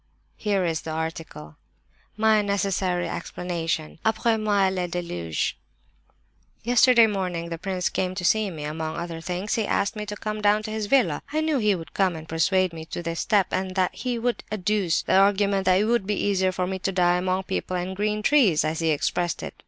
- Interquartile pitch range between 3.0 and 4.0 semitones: Yes, average, 3.6 semitones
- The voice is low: No, high, 190 Hz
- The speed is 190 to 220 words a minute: Yes, average, 200 wpm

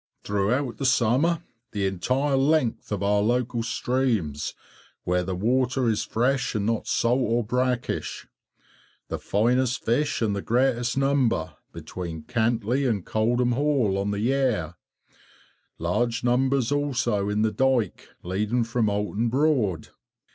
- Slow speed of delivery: Yes, slow, 130 wpm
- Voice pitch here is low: Yes, low, 120 Hz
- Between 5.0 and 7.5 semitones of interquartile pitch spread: No, average, 4.0 semitones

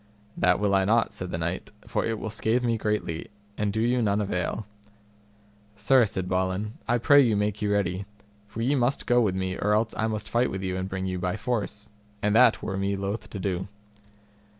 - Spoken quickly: Yes, fast, 215 wpm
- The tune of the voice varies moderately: Yes, average, 3.1 semitones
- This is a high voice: No, low, 105 Hz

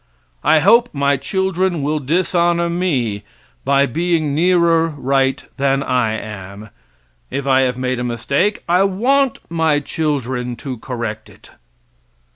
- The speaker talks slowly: Yes, slow, 130 wpm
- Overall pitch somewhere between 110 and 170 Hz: Yes, medium, 140 Hz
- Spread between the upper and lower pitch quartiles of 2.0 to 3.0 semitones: No, average, 5.3 semitones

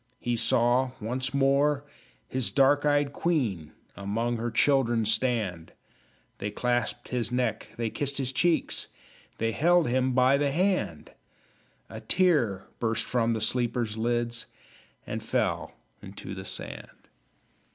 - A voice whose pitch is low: Yes, low, 125 Hz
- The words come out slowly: Yes, slow, 130 wpm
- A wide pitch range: No, average, 3.4 semitones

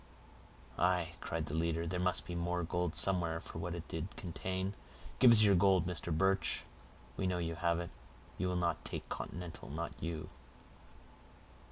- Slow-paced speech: No, average, 165 wpm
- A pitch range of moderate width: No, narrow, 1.8 semitones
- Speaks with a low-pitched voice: Yes, very low, 85 Hz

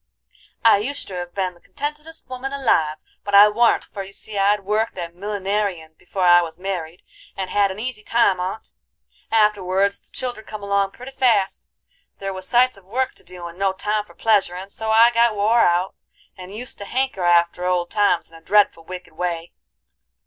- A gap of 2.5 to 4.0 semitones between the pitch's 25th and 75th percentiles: Yes, average, 3.5 semitones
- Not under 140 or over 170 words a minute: No, average, 190 wpm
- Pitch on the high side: Yes, high, 200 Hz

